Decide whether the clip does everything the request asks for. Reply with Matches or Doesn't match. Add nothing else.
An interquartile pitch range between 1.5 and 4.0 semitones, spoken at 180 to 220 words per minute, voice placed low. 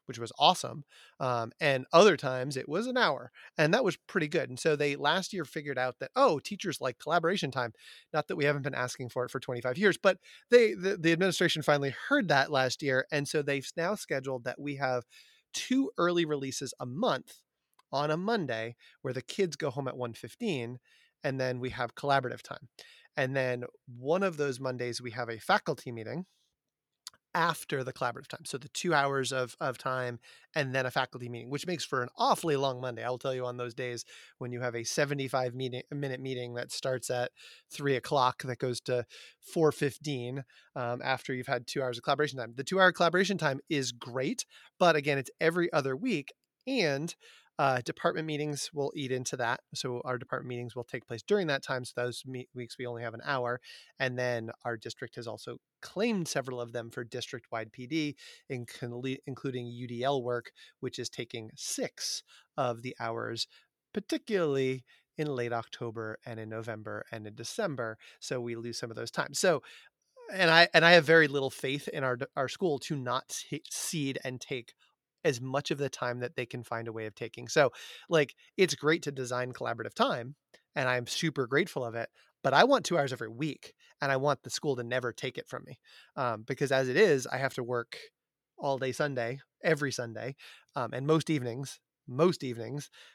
Matches